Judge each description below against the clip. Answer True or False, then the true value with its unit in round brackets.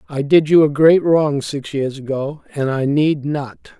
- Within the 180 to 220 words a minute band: True (205 wpm)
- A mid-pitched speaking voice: True (145 Hz)